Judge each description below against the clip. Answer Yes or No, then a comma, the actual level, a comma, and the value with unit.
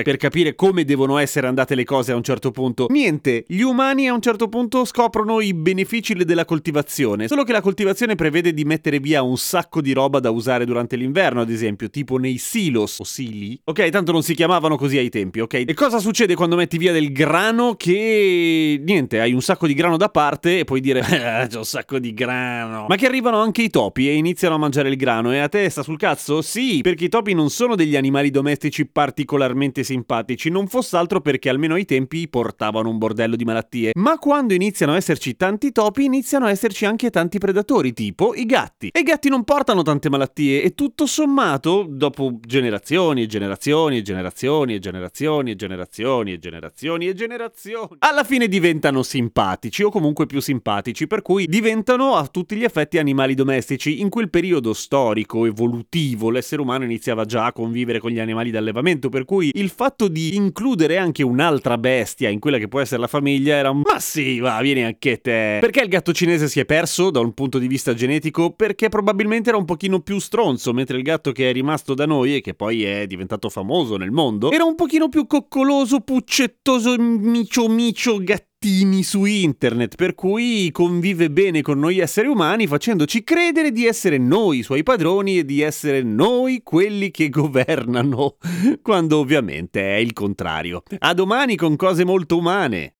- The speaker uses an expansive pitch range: Yes, wide, 7.7 semitones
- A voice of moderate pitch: Yes, medium, 155 Hz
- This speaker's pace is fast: Yes, fast, 195 wpm